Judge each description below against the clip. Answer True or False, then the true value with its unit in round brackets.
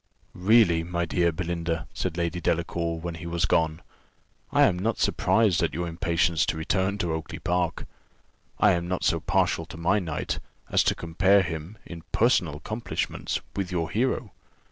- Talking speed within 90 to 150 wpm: False (165 wpm)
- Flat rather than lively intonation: True (2.1 semitones)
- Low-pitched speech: True (85 Hz)